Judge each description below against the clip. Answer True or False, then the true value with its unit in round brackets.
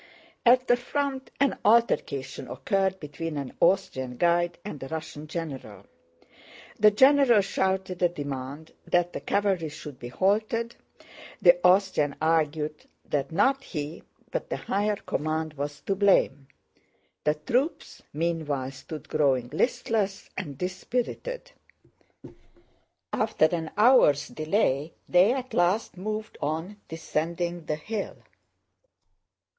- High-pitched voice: False (170 Hz)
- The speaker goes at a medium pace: False (120 wpm)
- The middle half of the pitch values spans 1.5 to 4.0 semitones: False (5.6 semitones)